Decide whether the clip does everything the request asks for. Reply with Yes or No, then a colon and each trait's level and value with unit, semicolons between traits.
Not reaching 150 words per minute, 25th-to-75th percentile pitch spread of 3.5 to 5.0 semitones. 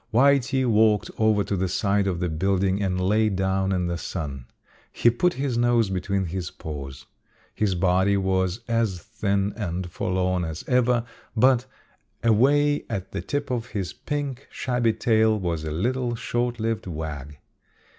No: average, 155 wpm; average, 4.5 semitones